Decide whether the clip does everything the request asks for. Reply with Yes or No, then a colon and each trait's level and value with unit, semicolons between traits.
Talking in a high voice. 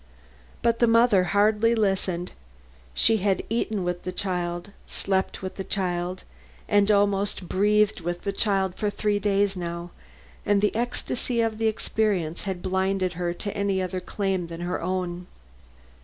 Yes: high, 195 Hz